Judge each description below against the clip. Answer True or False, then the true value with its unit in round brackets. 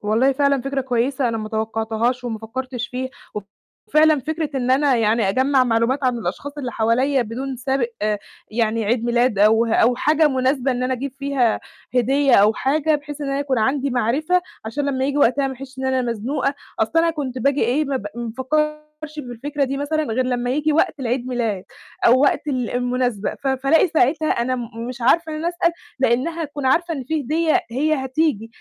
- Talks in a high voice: True (260 Hz)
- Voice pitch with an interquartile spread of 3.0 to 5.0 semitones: True (3.3 semitones)